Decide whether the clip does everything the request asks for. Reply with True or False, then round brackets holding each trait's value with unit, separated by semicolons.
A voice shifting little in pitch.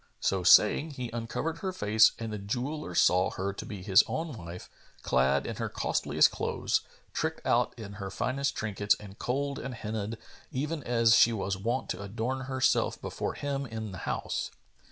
False (4.9 semitones)